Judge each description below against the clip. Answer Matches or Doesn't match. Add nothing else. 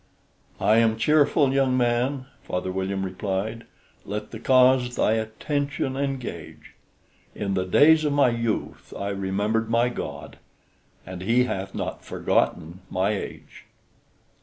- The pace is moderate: Doesn't match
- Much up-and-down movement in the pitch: Doesn't match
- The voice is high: Doesn't match